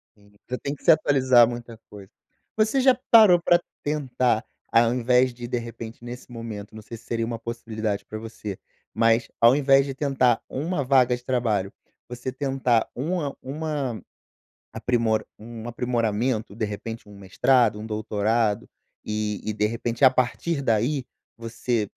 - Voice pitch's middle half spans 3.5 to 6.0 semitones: No, average, 2.9 semitones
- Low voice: Yes, low, 120 Hz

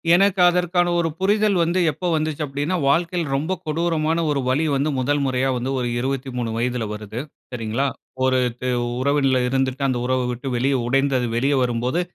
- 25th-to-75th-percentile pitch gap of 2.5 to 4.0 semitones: No, average, 4.5 semitones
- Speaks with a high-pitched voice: No, medium, 140 Hz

